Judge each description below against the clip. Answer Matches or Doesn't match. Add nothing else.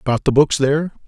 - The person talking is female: Doesn't match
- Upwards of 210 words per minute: Matches